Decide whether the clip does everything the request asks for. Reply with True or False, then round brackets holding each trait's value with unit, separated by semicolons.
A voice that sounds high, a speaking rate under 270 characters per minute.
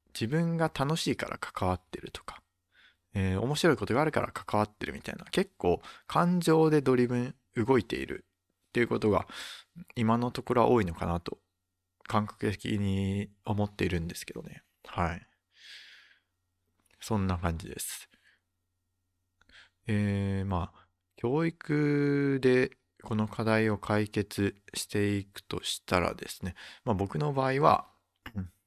False (105 Hz; 255 characters per minute)